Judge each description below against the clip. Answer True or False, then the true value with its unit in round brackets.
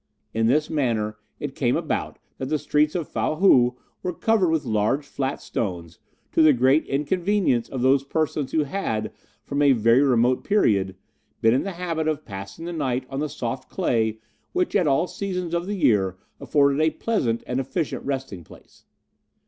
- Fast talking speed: False (180 wpm)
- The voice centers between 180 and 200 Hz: False (140 Hz)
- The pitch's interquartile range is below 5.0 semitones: False (5.3 semitones)